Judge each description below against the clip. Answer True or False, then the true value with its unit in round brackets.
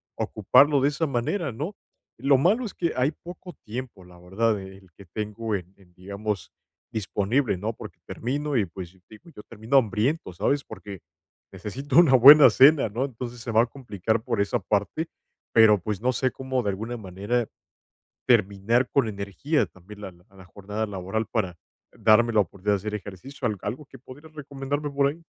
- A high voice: False (115 Hz)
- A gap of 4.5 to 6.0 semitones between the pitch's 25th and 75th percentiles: True (5.2 semitones)